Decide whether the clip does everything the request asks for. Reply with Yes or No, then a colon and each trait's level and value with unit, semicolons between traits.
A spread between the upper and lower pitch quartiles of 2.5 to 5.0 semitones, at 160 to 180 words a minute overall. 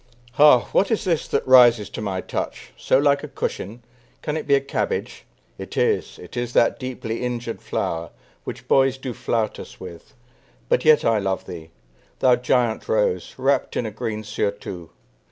Yes: average, 4.2 semitones; average, 175 wpm